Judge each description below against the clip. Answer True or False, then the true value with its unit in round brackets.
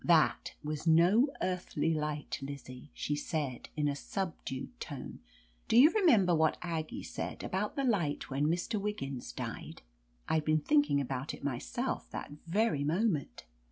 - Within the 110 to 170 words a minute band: True (150 wpm)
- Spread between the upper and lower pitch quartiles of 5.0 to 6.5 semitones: True (5.4 semitones)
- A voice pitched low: False (160 Hz)